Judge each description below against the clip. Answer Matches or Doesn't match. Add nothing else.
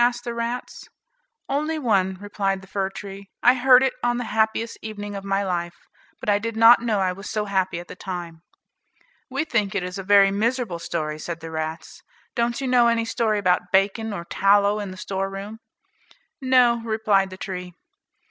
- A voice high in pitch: Matches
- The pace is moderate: Matches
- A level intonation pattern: Doesn't match